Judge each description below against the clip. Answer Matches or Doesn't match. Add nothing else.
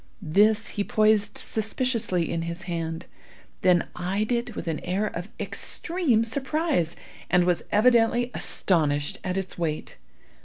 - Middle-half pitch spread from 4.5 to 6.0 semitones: Matches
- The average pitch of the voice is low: Doesn't match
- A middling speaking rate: Doesn't match